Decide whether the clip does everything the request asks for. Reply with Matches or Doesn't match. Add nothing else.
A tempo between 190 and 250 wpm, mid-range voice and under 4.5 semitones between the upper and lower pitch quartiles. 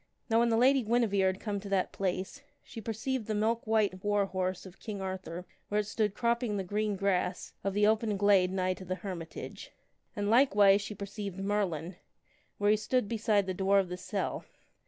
Doesn't match